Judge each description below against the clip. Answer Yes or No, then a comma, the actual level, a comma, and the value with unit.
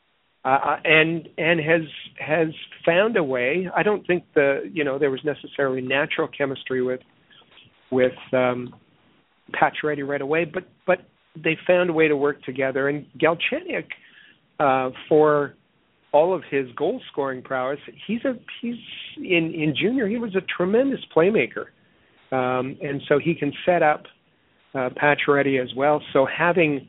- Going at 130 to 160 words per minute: Yes, average, 150 wpm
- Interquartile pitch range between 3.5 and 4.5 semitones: Yes, average, 4.0 semitones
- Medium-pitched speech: Yes, medium, 150 Hz